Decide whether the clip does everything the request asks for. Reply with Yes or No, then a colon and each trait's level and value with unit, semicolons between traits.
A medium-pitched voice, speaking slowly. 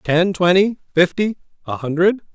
Yes: medium, 180 Hz; slow, 130 wpm